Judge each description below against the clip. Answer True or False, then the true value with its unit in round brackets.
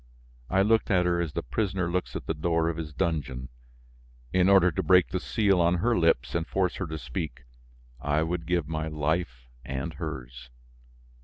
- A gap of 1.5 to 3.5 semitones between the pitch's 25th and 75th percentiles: True (3.0 semitones)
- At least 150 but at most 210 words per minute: True (185 wpm)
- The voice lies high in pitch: False (85 Hz)